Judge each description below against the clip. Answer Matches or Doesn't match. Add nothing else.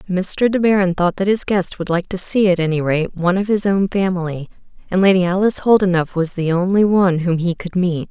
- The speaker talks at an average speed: Doesn't match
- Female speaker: Matches